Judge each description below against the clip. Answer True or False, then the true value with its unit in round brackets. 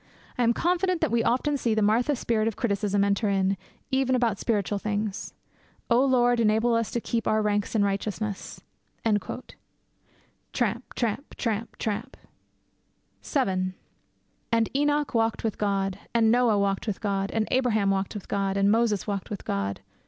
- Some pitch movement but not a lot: True (3.0 semitones)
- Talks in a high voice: True (220 Hz)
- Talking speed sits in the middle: True (160 wpm)